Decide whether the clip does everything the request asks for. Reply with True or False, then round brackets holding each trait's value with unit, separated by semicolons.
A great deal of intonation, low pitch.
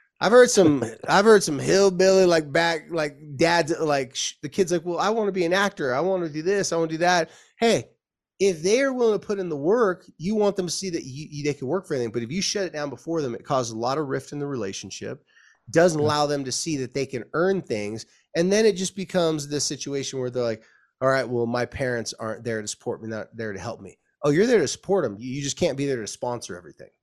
False (6.3 semitones; 155 Hz)